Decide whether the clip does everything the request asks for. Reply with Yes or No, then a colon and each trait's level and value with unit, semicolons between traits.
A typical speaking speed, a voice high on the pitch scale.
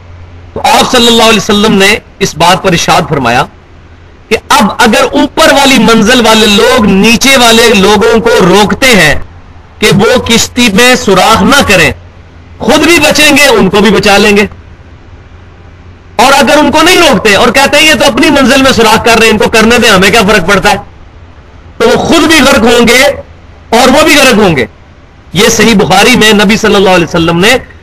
No: fast, 195 wpm; high, 215 Hz